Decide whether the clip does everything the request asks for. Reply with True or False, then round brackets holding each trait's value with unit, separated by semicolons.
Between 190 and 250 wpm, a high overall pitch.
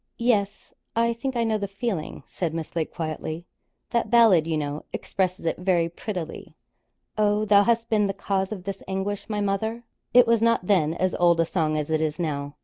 True (200 wpm; 195 Hz)